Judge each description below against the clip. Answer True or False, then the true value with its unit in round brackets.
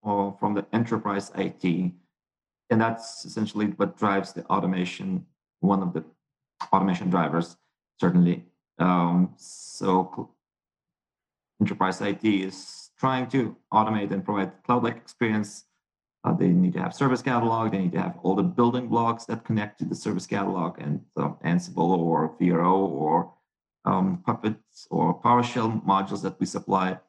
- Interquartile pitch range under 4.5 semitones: True (4.0 semitones)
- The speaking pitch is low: True (100 Hz)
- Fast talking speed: False (145 wpm)